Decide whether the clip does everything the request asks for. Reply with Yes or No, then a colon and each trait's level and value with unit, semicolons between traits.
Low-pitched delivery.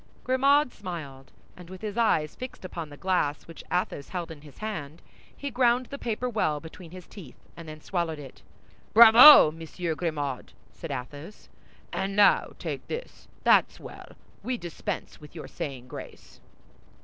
No: medium, 175 Hz